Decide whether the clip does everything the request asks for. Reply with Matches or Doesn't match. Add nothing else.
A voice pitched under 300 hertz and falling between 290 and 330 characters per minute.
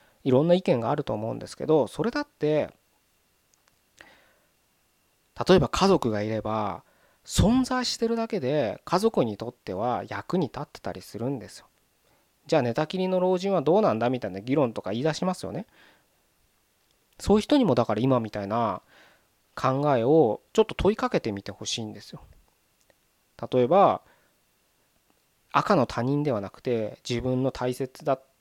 Matches